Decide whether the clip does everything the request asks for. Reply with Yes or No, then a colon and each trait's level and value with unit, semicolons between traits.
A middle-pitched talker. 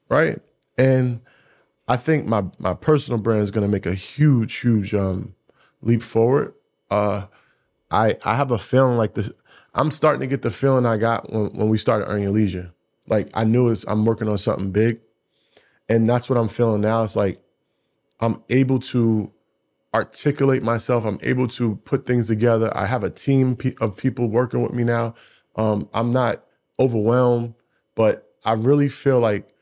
No: low, 115 Hz